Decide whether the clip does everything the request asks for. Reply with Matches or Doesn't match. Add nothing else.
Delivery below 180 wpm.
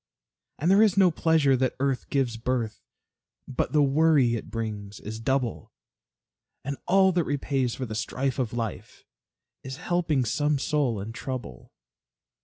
Matches